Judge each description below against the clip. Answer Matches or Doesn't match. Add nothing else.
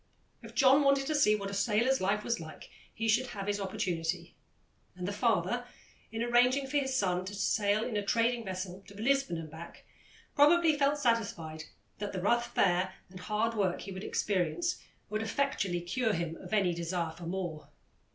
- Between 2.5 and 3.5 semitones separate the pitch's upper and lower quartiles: Doesn't match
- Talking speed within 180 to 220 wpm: Matches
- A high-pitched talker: Matches